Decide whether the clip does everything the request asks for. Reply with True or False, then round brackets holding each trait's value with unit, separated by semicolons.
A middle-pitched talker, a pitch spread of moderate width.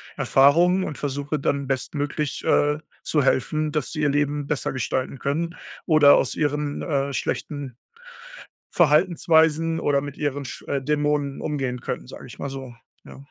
False (145 Hz; 1.8 semitones)